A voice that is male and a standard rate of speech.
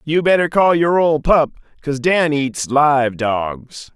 Yes: male; average, 165 wpm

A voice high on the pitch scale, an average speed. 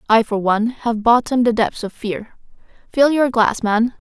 Yes: high, 230 Hz; average, 190 wpm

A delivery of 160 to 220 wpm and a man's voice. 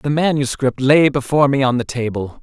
Yes: average, 200 wpm; male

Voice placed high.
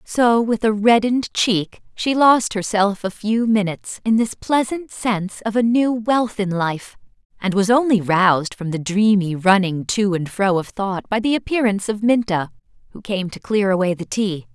Yes: high, 210 Hz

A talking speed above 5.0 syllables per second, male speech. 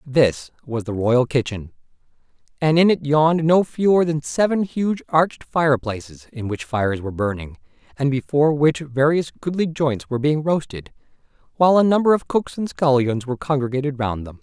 Yes: 5.4 syllables/s; male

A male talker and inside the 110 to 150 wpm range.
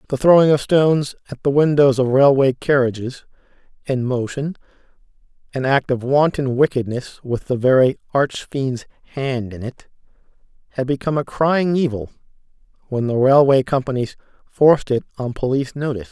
Yes: male; average, 140 wpm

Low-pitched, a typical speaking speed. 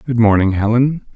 Yes: low, 115 Hz; average, 155 wpm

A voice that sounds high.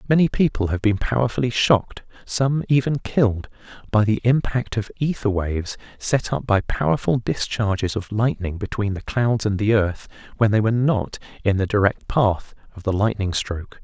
No: low, 110 Hz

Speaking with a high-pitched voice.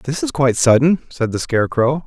No: low, 135 Hz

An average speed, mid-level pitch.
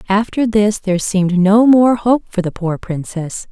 No: average, 190 wpm; high, 200 Hz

